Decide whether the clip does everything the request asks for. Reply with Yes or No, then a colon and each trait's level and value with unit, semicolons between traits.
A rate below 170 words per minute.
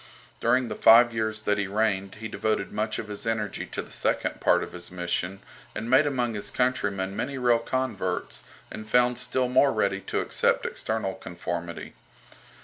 No: average, 175 wpm